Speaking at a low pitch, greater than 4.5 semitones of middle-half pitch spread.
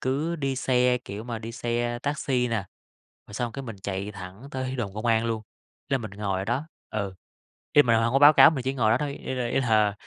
No: low, 120 Hz; average, 3.6 semitones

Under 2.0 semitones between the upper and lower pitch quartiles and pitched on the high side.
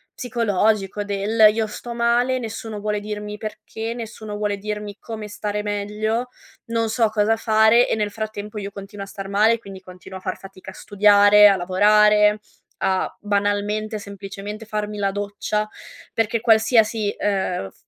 Yes: narrow, 1.4 semitones; high, 210 Hz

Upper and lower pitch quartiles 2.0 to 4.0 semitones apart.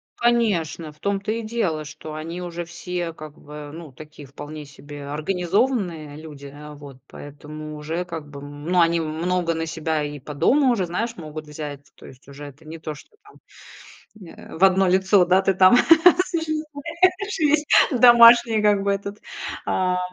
No: wide, 5.5 semitones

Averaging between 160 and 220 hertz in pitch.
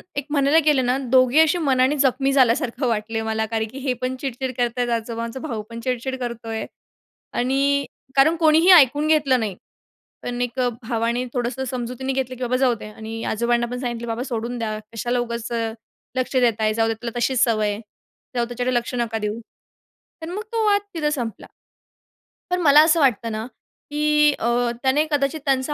No: very high, 250 Hz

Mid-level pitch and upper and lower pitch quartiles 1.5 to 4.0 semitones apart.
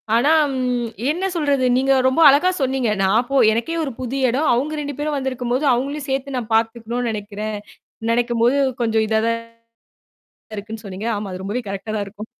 No: high, 245 Hz; average, 3.7 semitones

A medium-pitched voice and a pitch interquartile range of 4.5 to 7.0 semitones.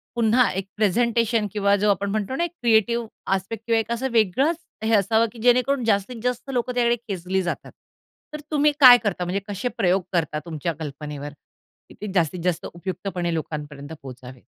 No: high, 205 Hz; average, 5.2 semitones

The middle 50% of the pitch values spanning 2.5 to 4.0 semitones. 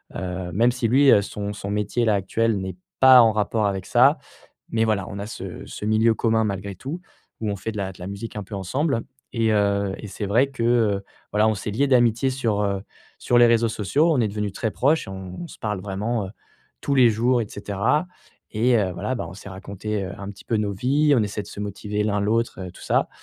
Yes: average, 2.8 semitones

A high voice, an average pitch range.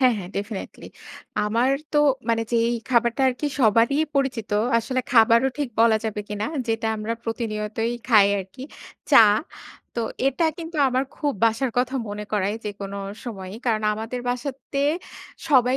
Yes: high, 230 Hz; average, 3.3 semitones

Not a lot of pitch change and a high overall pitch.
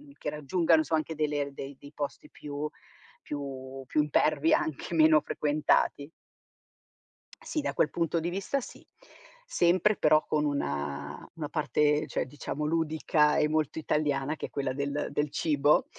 No: narrow, 1.8 semitones; medium, 150 Hz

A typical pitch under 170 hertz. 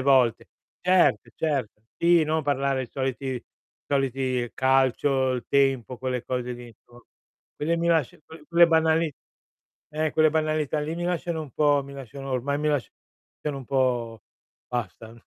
Yes: low, 135 Hz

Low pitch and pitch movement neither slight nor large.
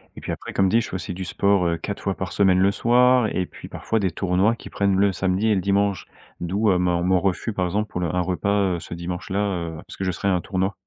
No: very low, 95 Hz; narrow, 2.0 semitones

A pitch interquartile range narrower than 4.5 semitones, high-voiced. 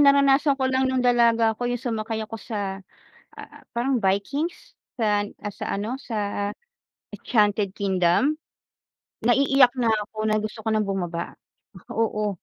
Yes: average, 3.6 semitones; high, 220 Hz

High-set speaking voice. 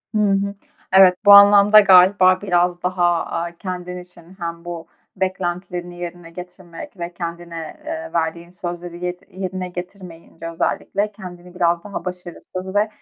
No: medium, 180 Hz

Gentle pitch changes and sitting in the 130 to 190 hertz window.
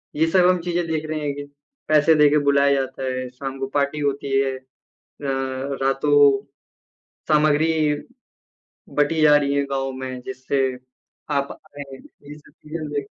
Yes: narrow, 1.9 semitones; medium, 140 Hz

